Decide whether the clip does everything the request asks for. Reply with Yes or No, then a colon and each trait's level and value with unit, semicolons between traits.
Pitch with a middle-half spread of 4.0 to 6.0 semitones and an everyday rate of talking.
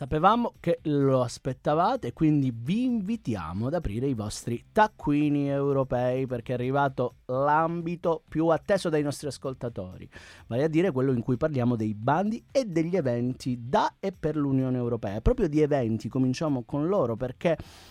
Yes: average, 4.7 semitones; average, 160 wpm